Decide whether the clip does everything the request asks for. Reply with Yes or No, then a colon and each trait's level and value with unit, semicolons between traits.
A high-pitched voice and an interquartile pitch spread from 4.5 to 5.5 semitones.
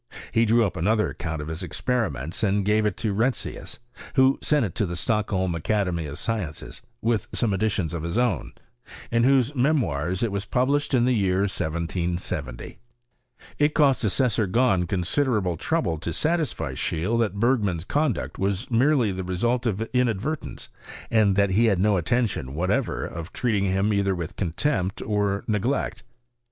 No: low, 105 Hz; average, 4.9 semitones